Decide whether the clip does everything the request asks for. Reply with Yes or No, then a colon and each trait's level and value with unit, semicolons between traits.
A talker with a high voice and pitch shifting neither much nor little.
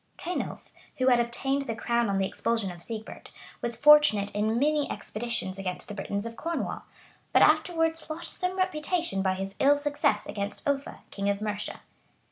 No: high, 235 Hz; wide, 6.7 semitones